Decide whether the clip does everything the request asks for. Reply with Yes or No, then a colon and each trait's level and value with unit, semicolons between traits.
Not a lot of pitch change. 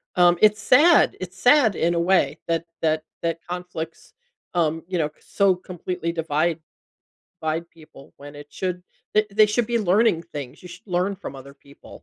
No: average, 3.5 semitones